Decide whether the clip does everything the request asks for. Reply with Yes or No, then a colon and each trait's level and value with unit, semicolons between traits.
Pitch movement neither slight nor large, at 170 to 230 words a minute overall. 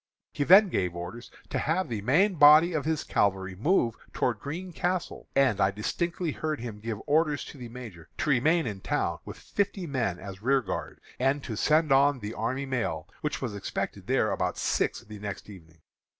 No: wide, 7.0 semitones; average, 190 wpm